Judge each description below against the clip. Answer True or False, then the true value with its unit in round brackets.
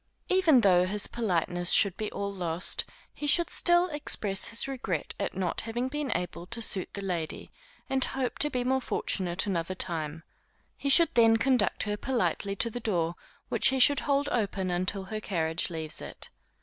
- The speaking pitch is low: False (210 Hz)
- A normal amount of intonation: False (6.5 semitones)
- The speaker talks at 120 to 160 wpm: False (180 wpm)